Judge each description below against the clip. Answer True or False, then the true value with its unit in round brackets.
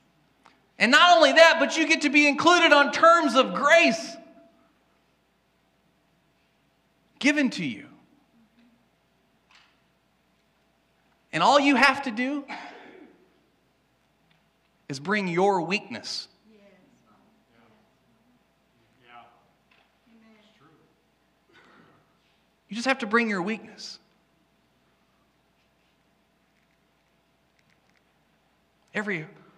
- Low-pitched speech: False (235 Hz)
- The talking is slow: True (70 wpm)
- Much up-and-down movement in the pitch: True (5.7 semitones)